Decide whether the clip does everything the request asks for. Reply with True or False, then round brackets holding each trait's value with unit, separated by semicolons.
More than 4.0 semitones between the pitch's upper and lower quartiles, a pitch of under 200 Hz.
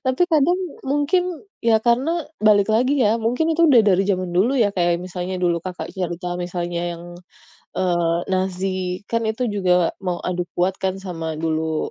True (5.0 semitones; 190 Hz)